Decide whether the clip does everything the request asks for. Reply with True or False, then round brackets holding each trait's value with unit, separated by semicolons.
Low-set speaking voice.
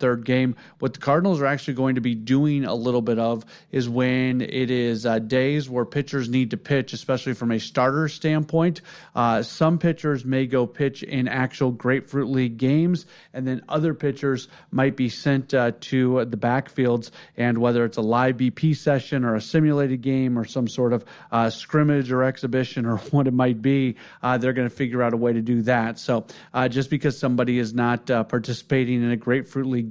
True (130 Hz)